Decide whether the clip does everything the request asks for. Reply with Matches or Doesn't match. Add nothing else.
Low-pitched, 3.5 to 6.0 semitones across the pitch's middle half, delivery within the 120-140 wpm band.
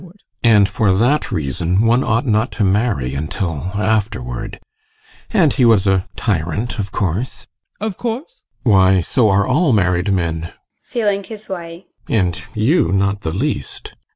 Doesn't match